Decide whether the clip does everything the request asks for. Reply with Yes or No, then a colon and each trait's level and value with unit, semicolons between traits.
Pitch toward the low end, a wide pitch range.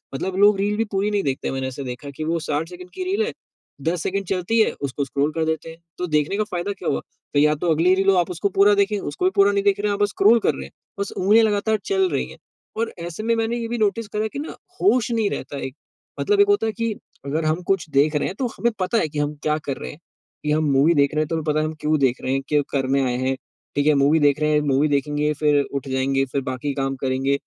No: medium, 160 Hz; wide, 6.3 semitones